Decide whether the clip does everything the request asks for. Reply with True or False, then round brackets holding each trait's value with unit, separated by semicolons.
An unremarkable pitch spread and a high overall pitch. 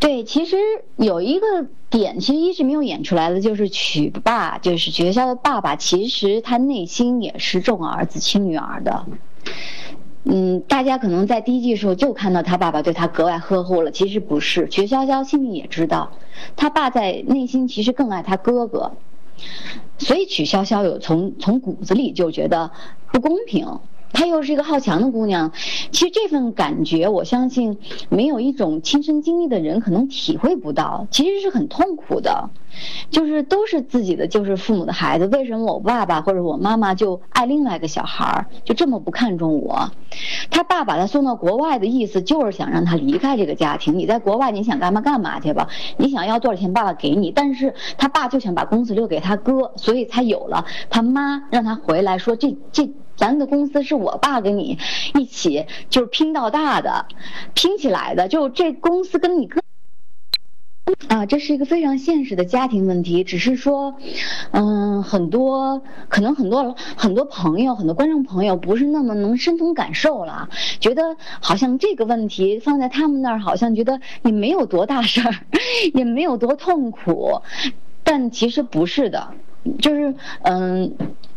False (6.6 semitones; 245 Hz)